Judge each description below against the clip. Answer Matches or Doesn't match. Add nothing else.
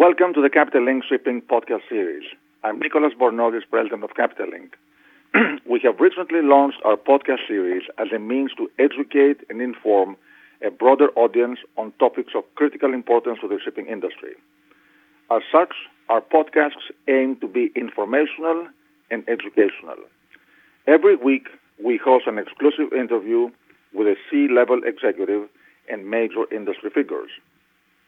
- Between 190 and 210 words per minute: Doesn't match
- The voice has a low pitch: Doesn't match